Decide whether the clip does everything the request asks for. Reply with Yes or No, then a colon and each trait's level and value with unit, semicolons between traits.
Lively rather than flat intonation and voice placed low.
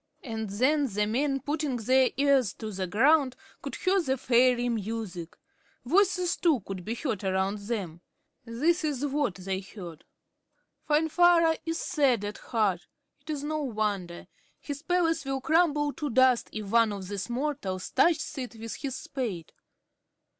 No: wide, 6.2 semitones; very high, 250 Hz